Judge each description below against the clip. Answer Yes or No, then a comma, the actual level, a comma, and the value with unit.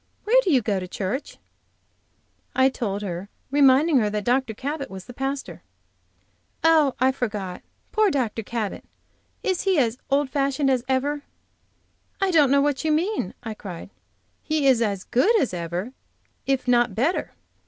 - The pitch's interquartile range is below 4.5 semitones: No, wide, 5.4 semitones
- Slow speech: No, average, 160 wpm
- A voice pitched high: Yes, very high, 260 Hz